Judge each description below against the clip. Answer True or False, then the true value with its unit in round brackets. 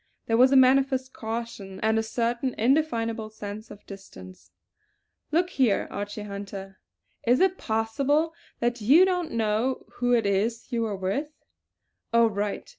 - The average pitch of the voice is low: False (230 Hz)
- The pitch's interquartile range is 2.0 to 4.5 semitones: True (4.0 semitones)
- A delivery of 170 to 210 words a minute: False (150 wpm)